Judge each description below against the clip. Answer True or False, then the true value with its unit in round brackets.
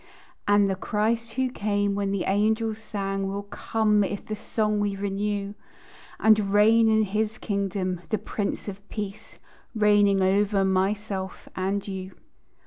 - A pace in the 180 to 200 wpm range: False (140 wpm)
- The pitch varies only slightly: True (1.5 semitones)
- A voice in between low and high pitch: False (205 Hz)